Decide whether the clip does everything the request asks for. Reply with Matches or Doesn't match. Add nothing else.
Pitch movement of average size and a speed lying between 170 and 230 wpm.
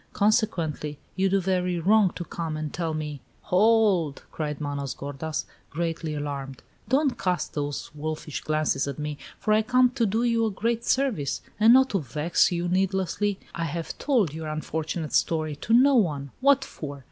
Doesn't match